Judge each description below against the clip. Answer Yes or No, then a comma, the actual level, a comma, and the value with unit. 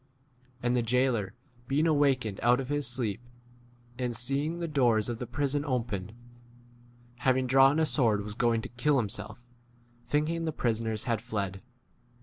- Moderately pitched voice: No, low, 125 Hz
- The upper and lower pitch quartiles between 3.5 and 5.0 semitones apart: Yes, average, 3.8 semitones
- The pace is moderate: Yes, average, 160 wpm